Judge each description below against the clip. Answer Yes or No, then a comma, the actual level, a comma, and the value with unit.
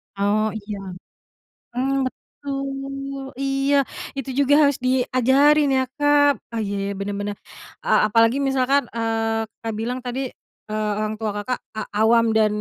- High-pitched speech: Yes, high, 245 Hz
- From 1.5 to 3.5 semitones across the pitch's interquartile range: No, average, 4.0 semitones